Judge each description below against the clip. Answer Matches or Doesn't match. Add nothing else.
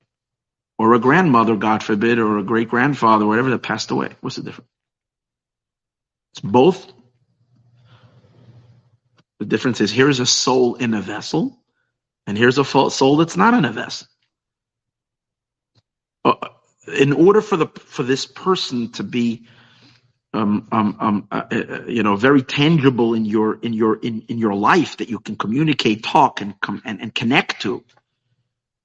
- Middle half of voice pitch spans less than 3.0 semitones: Matches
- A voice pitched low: Matches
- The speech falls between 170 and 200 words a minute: Doesn't match